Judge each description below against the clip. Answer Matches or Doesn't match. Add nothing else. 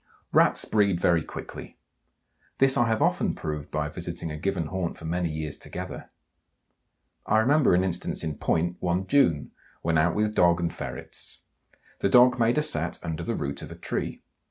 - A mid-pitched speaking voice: Doesn't match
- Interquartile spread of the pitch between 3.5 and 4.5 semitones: Doesn't match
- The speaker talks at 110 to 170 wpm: Doesn't match